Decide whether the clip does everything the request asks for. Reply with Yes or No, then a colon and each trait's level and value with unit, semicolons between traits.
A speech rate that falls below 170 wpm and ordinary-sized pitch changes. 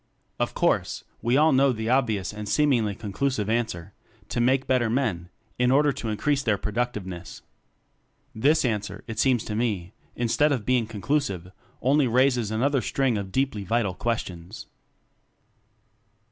Yes: average, 150 wpm; average, 4.2 semitones